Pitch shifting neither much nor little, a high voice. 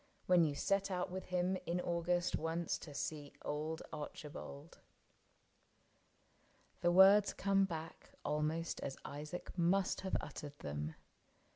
No: average, 3.3 semitones; medium, 170 Hz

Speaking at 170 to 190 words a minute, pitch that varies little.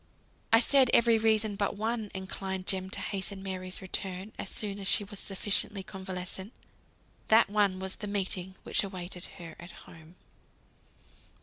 No: average, 150 wpm; narrow, 2.0 semitones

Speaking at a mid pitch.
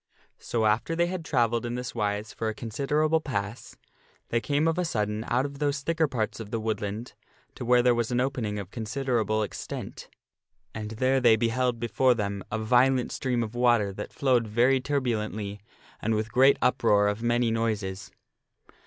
No: low, 120 Hz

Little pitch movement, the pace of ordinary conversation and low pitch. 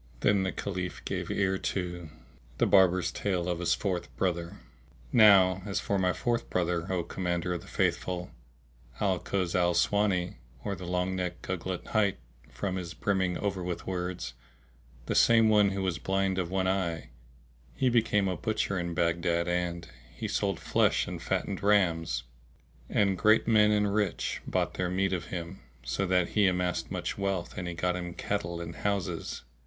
Yes: narrow, 2.1 semitones; average, 170 wpm; very low, 90 Hz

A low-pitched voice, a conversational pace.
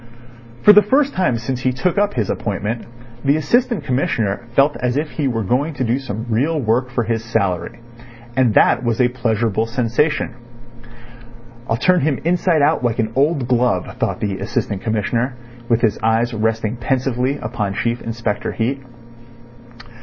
Yes: low, 120 Hz; average, 165 wpm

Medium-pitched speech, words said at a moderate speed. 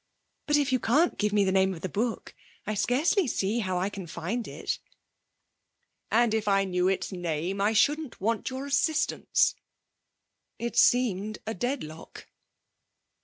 No: high, 215 Hz; average, 155 wpm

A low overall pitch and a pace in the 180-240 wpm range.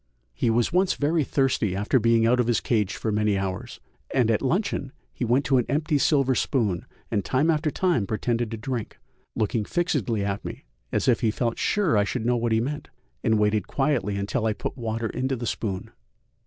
Yes: low, 115 Hz; fast, 205 wpm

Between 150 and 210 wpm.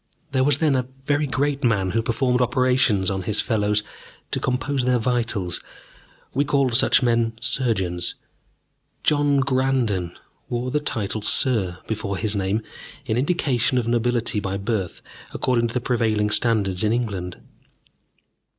No: average, 140 wpm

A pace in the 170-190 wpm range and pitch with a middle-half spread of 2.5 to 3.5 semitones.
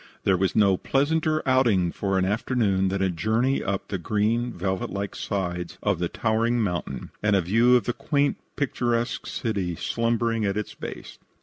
No: average, 175 wpm; average, 4.0 semitones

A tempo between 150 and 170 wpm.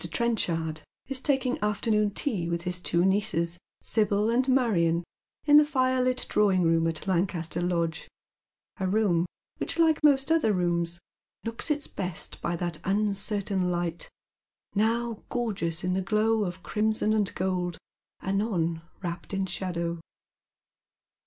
No: slow, 135 wpm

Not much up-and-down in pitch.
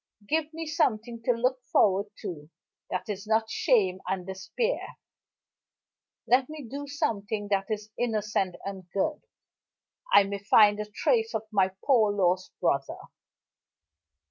No: average, 4.6 semitones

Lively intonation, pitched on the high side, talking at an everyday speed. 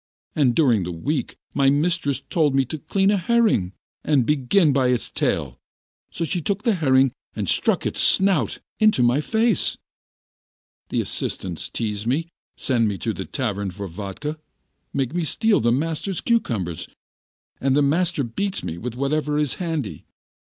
No: wide, 6.2 semitones; medium, 140 Hz; average, 165 wpm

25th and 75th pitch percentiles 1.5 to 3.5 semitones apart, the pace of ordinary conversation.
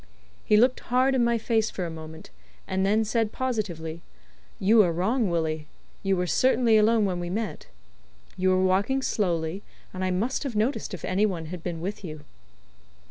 No: average, 4.4 semitones; average, 185 wpm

